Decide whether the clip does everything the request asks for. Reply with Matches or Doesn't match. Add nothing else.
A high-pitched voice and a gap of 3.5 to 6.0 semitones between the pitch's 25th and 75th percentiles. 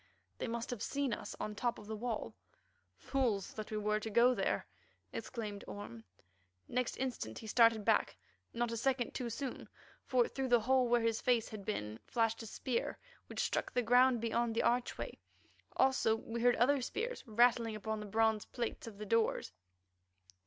Doesn't match